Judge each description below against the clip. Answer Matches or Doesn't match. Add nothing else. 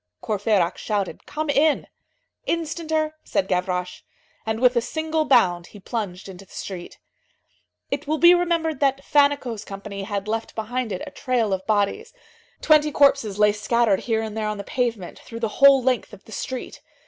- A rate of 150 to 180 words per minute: Matches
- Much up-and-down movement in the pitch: Matches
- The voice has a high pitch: Matches